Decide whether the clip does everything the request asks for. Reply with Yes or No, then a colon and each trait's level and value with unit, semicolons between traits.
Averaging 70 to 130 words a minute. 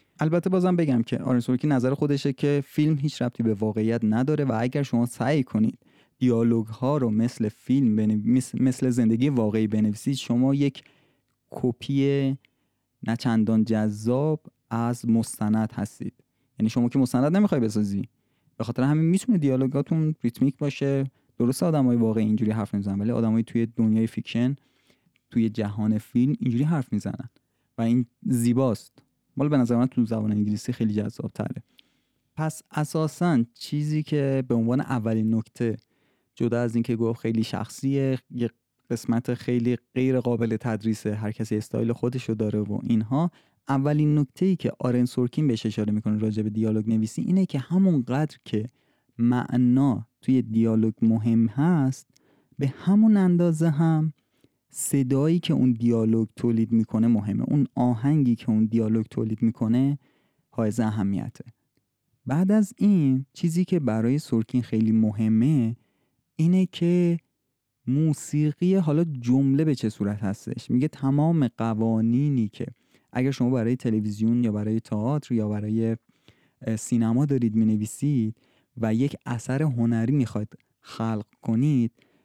No: average, 140 wpm